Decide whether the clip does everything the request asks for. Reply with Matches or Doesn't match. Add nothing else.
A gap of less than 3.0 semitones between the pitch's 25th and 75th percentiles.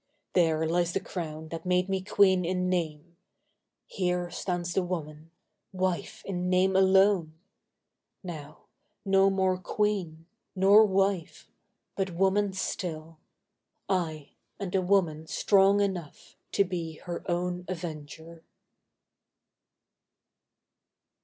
Matches